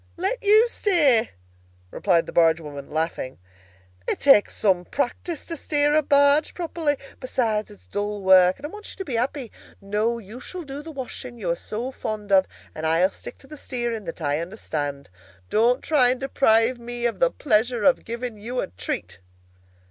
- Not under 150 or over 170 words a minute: No, average, 185 wpm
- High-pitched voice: Yes, high, 235 Hz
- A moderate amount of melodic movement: No, wide, 6.9 semitones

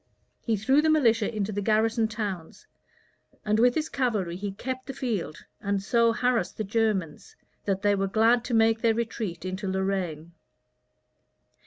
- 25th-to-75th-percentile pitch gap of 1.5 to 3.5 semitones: Yes, average, 3.2 semitones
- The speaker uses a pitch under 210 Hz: No, high, 215 Hz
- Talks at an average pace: Yes, average, 160 wpm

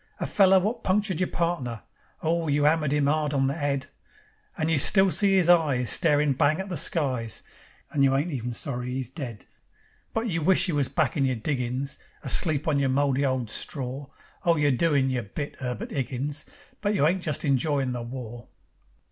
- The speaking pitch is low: No, medium, 145 Hz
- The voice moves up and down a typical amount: Yes, average, 4.0 semitones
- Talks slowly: No, average, 190 wpm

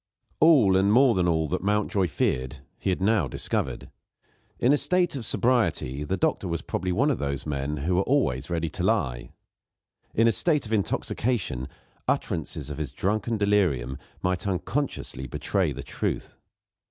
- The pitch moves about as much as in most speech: No, wide, 7.5 semitones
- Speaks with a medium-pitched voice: No, very low, 95 Hz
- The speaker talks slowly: No, average, 165 wpm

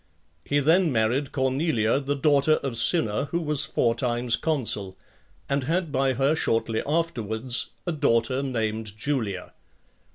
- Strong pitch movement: No, average, 4.4 semitones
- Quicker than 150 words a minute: No, average, 140 wpm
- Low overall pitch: Yes, low, 130 Hz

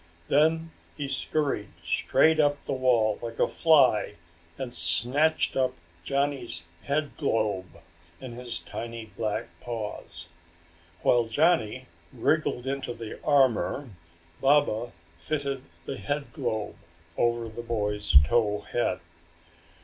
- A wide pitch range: No, average, 4.6 semitones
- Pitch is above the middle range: No, low, 120 Hz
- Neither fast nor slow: No, slow, 105 wpm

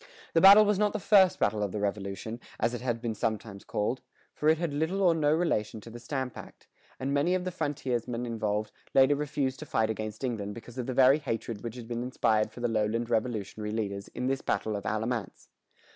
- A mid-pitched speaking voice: No, low, 120 Hz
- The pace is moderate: No, fast, 220 wpm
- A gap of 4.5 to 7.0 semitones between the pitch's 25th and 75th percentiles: Yes, average, 4.8 semitones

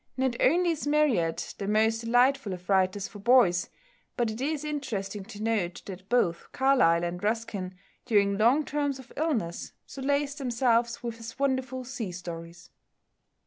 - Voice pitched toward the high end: Yes, high, 230 Hz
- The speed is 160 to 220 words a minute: No, average, 150 wpm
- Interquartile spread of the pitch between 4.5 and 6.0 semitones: Yes, average, 5.3 semitones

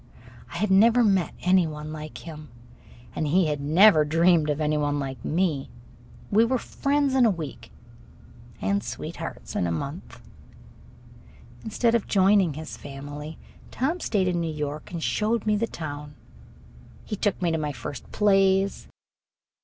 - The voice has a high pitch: No, medium, 165 Hz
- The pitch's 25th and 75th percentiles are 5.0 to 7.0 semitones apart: Yes, wide, 5.5 semitones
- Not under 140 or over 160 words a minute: Yes, average, 155 wpm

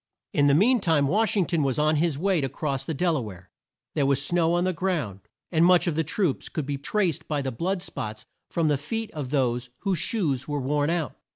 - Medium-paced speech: No, fast, 245 wpm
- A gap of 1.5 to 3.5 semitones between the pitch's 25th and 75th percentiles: No, average, 4.3 semitones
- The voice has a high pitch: No, medium, 155 Hz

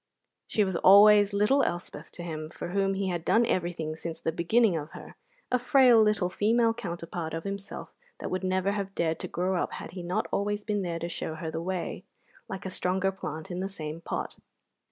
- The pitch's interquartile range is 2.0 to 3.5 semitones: Yes, average, 3.2 semitones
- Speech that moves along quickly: Yes, fast, 210 wpm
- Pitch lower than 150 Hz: No, medium, 185 Hz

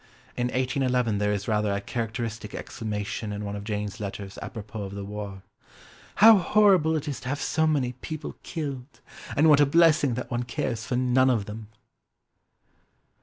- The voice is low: Yes, low, 120 Hz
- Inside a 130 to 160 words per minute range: No, average, 170 wpm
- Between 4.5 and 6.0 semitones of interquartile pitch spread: Yes, average, 5.2 semitones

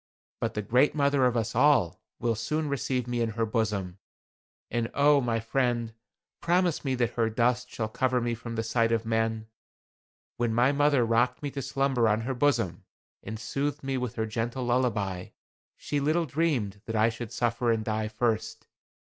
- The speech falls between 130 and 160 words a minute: No, average, 180 wpm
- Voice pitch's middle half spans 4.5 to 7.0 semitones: No, average, 3.1 semitones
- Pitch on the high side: No, low, 120 Hz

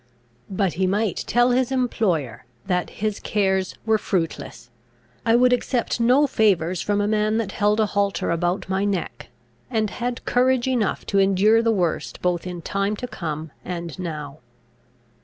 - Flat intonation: No, average, 4.1 semitones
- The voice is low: No, high, 200 Hz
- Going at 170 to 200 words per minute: No, average, 160 wpm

